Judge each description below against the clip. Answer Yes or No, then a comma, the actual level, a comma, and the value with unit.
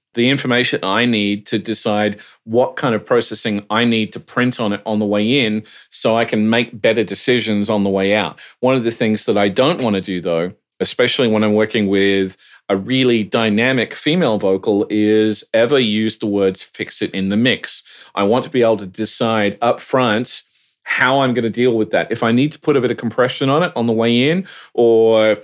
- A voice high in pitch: No, low, 110 Hz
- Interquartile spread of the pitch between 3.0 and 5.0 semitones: No, narrow, 2.6 semitones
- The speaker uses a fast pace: Yes, fast, 220 wpm